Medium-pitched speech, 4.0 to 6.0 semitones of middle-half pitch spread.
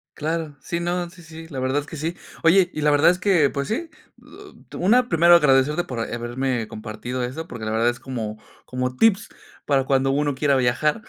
Yes: medium, 145 Hz; average, 5.0 semitones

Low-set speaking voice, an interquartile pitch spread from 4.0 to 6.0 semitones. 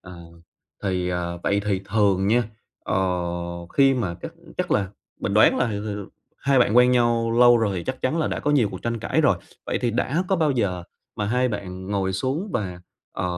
Yes: low, 105 Hz; average, 4.7 semitones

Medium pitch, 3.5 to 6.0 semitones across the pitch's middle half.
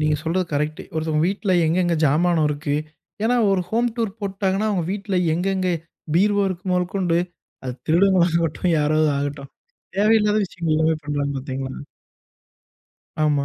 Yes: medium, 170 Hz; average, 4.2 semitones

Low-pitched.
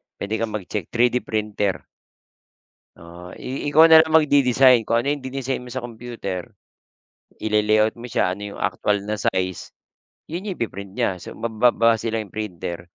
Yes: low, 110 Hz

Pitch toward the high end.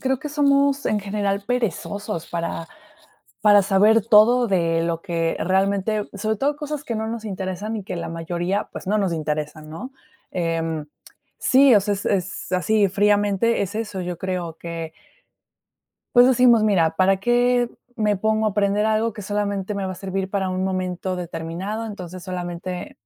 Yes: high, 200 Hz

